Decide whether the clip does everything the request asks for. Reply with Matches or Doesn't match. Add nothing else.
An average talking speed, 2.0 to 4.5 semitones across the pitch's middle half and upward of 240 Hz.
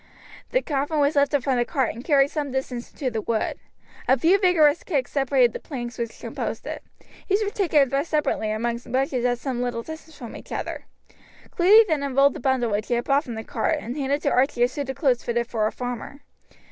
Doesn't match